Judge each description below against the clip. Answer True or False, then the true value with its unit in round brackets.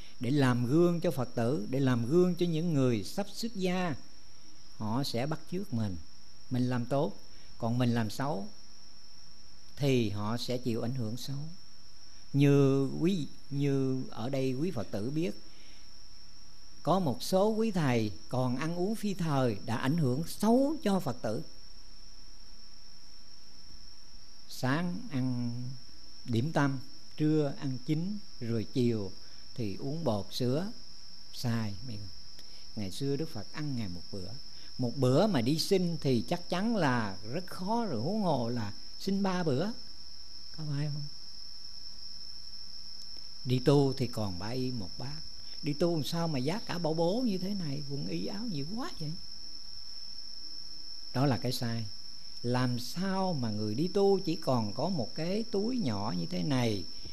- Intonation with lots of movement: True (7.2 semitones)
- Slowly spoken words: True (155 wpm)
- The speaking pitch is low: True (130 Hz)